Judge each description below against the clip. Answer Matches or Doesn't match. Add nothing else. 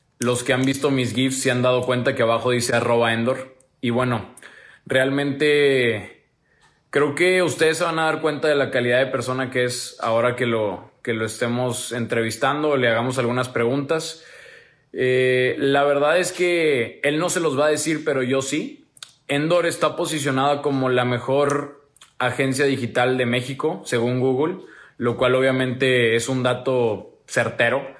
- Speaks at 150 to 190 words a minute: Matches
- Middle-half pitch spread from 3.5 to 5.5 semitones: Doesn't match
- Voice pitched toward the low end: Matches